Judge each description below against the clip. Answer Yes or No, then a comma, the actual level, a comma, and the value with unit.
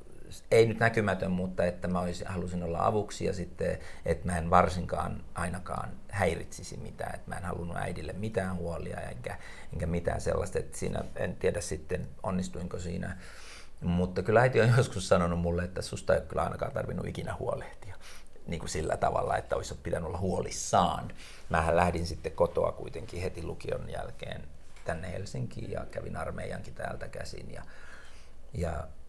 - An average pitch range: No, narrow, 1.5 semitones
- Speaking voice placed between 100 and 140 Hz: No, very low, 90 Hz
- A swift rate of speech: Yes, fast, 165 wpm